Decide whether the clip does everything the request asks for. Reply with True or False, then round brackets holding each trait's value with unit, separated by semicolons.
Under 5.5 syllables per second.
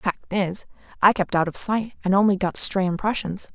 True (4.9 syllables/s)